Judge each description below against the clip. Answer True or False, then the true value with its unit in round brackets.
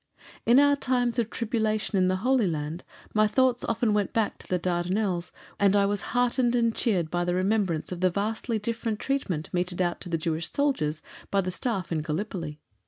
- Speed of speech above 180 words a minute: True (195 wpm)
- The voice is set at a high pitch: True (200 Hz)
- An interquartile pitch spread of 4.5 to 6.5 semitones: True (4.8 semitones)